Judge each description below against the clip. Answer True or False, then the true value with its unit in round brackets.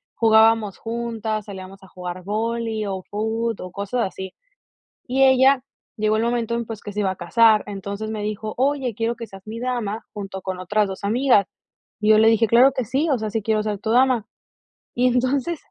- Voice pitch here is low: False (220 Hz)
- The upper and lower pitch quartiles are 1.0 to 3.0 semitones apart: True (2.6 semitones)